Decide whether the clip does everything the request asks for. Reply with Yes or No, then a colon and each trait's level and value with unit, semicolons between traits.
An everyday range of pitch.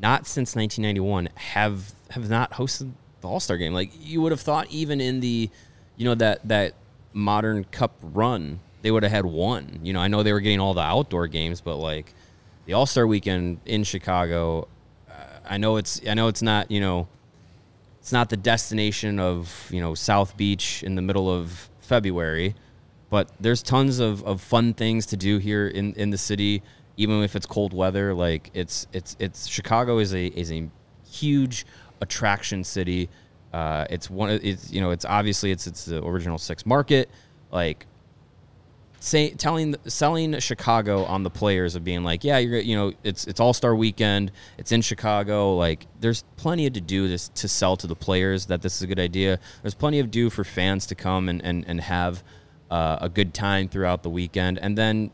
Yes: average, 3.9 semitones